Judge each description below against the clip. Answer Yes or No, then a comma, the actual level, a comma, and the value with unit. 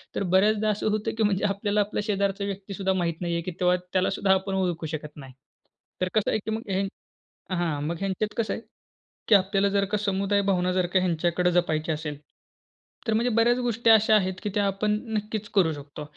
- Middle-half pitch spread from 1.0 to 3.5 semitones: Yes, average, 2.9 semitones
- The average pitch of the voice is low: No, high, 195 Hz